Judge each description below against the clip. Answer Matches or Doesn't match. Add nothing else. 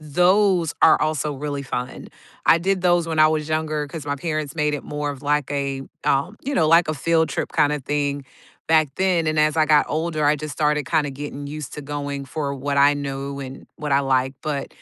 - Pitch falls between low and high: Matches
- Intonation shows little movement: Matches